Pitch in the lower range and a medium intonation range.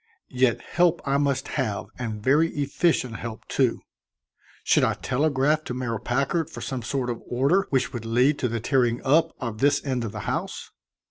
Yes: low, 130 Hz; average, 3.3 semitones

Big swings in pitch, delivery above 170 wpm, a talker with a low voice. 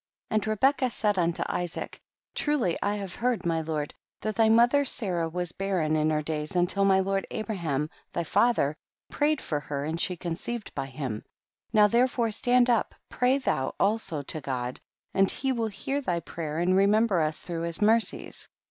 No: wide, 5.9 semitones; average, 185 wpm; high, 190 Hz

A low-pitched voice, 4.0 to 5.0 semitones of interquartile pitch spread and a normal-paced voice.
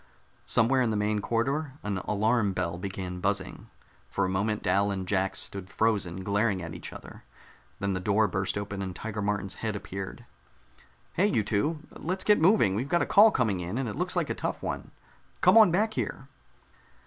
Yes: low, 105 Hz; average, 4.5 semitones; average, 195 wpm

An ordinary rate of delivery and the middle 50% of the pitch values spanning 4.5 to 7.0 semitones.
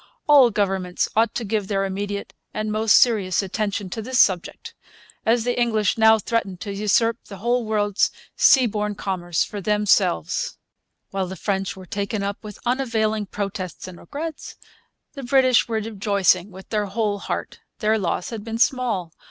No: average, 160 wpm; average, 2.7 semitones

